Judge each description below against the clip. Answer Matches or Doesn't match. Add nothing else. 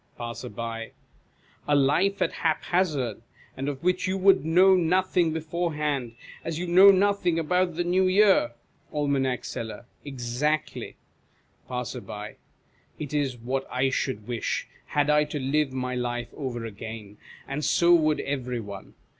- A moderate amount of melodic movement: Doesn't match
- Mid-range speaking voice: Matches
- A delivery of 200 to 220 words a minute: Doesn't match